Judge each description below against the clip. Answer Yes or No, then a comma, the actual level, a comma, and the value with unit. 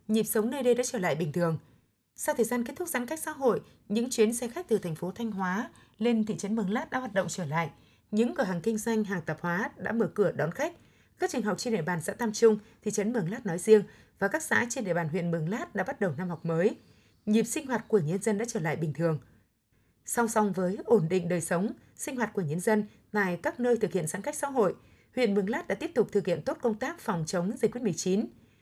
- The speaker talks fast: Yes, fast, 265 wpm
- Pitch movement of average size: Yes, average, 4.7 semitones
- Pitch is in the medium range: No, high, 210 Hz